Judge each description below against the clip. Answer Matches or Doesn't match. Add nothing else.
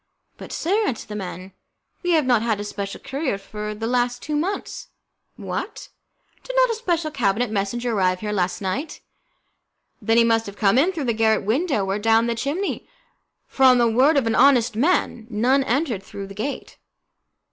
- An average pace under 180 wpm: Doesn't match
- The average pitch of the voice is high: Matches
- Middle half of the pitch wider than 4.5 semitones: Matches